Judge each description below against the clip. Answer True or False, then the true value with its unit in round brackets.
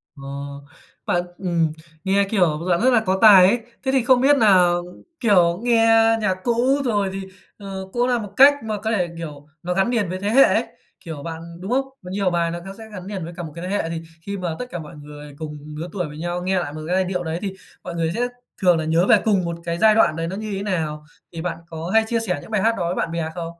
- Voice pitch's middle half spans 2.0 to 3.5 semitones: False (4.3 semitones)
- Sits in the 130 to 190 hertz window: True (185 Hz)